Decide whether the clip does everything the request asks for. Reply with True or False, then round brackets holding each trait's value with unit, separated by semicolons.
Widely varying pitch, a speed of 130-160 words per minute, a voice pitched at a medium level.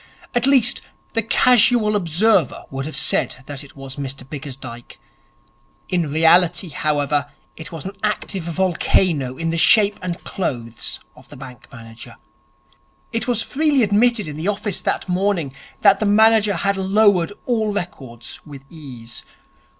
True (7.0 semitones; 145 wpm; 175 Hz)